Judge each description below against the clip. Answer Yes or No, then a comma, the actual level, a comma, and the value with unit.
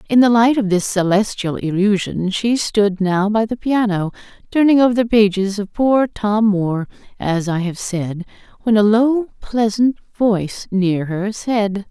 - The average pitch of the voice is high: Yes, high, 210 Hz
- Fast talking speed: No, average, 165 wpm